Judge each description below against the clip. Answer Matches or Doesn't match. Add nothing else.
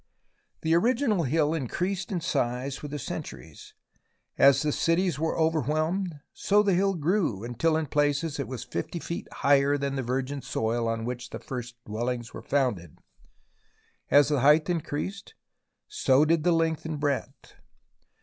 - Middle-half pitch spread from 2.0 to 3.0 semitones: Doesn't match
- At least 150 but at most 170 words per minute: Matches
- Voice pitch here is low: Doesn't match